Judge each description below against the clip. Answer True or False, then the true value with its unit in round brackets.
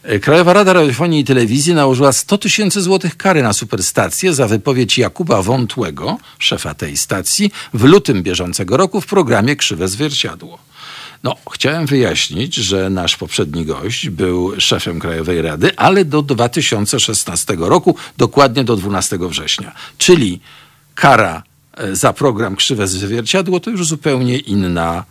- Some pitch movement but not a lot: False (8.4 semitones)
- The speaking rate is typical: True (135 wpm)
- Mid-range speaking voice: False (125 Hz)